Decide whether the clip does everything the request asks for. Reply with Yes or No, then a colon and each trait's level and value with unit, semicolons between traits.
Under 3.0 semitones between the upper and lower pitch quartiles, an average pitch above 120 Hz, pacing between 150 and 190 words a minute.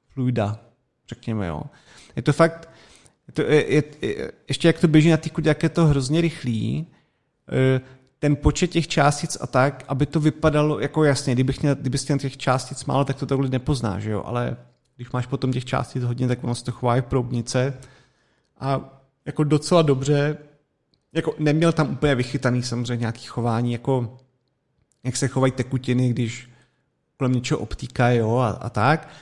No: average, 3.3 semitones; low, 135 Hz; fast, 170 wpm